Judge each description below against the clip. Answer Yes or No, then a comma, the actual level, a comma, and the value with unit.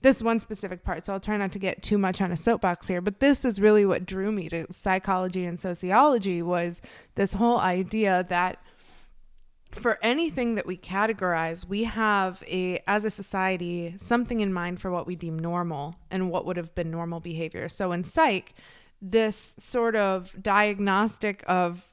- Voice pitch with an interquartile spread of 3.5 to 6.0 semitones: No, average, 3.1 semitones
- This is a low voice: No, high, 190 Hz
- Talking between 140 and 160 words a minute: No, average, 180 wpm